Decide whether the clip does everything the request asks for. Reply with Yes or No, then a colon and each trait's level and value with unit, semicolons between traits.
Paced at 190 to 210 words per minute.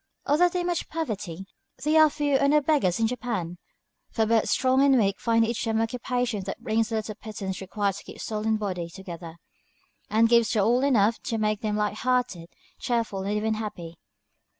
Yes: average, 195 wpm